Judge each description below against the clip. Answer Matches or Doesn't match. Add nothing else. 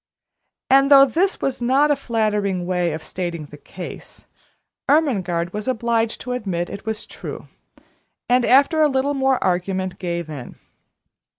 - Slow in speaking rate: Doesn't match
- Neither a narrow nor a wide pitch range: Doesn't match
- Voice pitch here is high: Matches